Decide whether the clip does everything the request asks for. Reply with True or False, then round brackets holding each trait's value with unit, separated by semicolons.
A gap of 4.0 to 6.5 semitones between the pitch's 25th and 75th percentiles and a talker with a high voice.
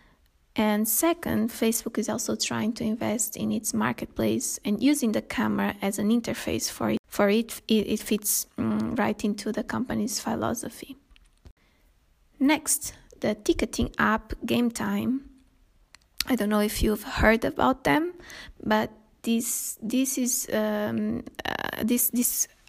False (2.9 semitones; 225 Hz)